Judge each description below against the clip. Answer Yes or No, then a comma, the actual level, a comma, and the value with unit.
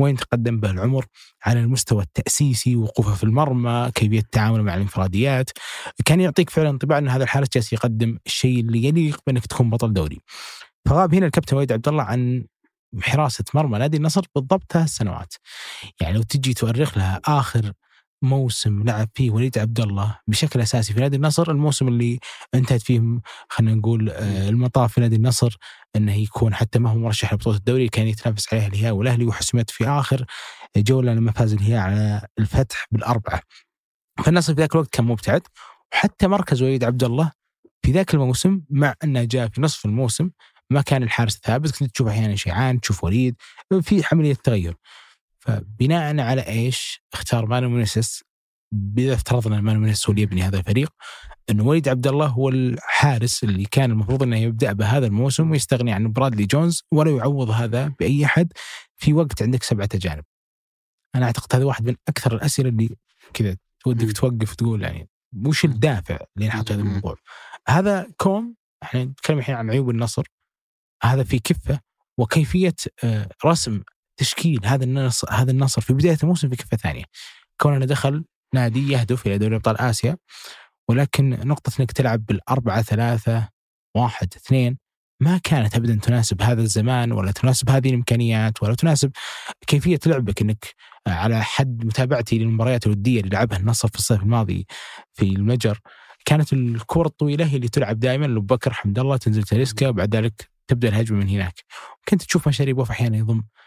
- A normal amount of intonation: Yes, average, 3.9 semitones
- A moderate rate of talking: No, fast, 160 wpm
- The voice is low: Yes, low, 120 Hz